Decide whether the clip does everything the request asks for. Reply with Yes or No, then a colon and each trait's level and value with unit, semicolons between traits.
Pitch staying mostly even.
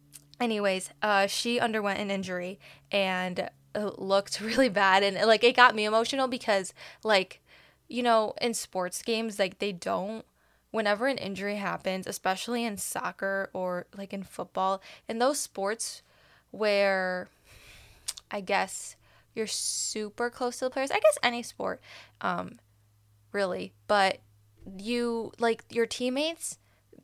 No: average, 3.9 semitones